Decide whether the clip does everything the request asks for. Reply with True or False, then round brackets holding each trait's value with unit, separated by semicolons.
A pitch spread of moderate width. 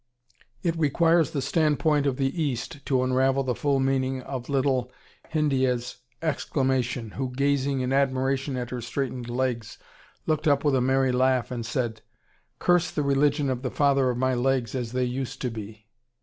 False (2.0 semitones)